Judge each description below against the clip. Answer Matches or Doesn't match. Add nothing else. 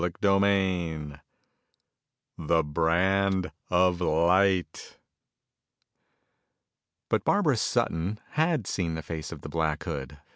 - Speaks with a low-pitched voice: Matches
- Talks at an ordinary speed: Doesn't match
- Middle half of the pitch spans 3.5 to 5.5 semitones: Doesn't match